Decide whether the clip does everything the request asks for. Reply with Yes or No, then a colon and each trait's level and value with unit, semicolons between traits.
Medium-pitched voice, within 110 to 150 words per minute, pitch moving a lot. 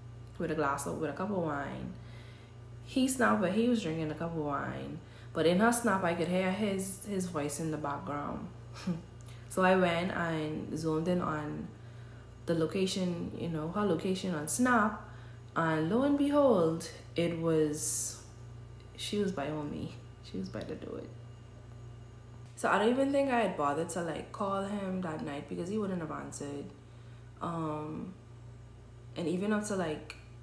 No: medium, 155 Hz; average, 175 wpm; wide, 7.5 semitones